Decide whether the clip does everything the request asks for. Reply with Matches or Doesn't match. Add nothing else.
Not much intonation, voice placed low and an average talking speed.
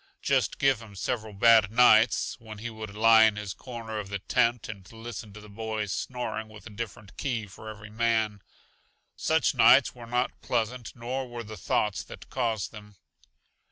Matches